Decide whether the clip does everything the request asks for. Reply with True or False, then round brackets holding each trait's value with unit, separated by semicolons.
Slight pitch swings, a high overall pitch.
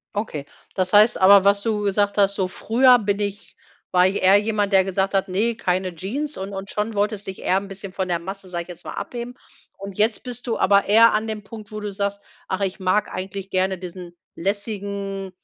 True (1.8 semitones; 200 Hz)